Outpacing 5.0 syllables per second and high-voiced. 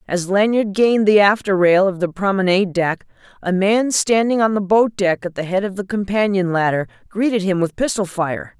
Yes: 5.2 syllables/s; high, 195 Hz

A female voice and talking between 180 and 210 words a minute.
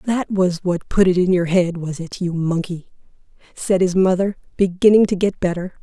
Yes: female; average, 195 wpm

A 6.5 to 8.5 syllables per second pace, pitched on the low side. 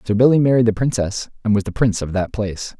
Yes: 6.9 syllables/s; low, 110 Hz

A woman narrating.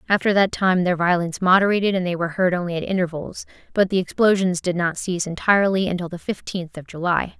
Yes: female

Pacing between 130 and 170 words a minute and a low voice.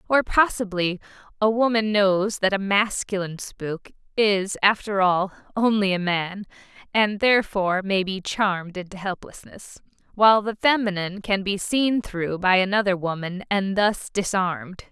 No: average, 140 wpm; high, 195 Hz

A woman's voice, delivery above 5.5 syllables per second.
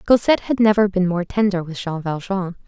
Yes: female; 5.7 syllables/s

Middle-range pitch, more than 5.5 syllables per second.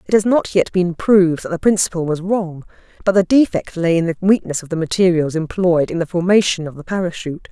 Yes: medium, 175 Hz; 5.9 syllables/s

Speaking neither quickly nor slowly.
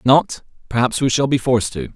No: fast, 245 wpm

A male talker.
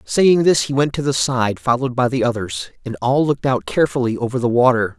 Yes: male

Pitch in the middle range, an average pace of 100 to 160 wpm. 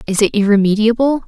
No: high, 220 Hz; average, 140 wpm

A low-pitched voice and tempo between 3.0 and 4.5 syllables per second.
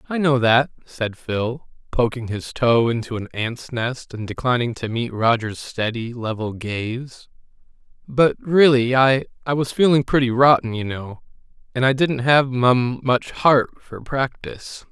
Yes: low, 125 Hz; 4.1 syllables/s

